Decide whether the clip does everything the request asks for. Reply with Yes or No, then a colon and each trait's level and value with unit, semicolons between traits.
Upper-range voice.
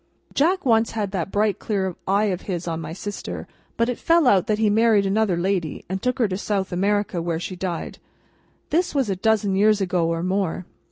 Yes: high, 200 Hz